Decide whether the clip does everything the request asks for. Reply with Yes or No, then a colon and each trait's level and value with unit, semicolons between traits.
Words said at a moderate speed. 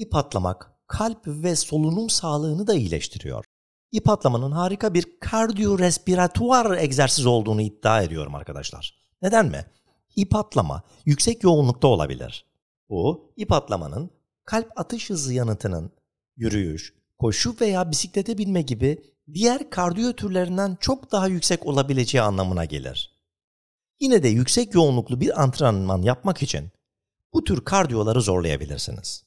Yes: average, 125 wpm